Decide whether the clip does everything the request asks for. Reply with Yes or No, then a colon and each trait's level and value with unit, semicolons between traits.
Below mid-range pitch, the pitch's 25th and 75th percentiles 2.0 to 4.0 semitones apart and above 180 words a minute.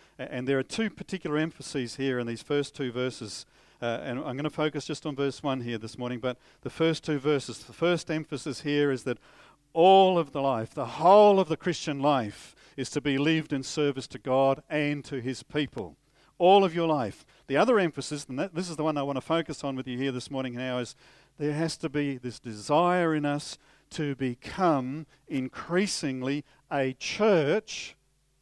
No: medium, 145 Hz; average, 3.2 semitones; average, 200 wpm